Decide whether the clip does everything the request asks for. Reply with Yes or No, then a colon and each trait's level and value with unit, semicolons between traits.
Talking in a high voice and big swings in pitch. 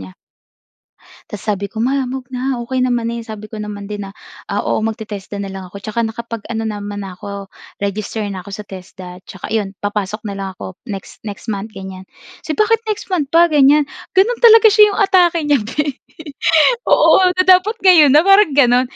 Yes: high, 225 Hz; wide, 6.9 semitones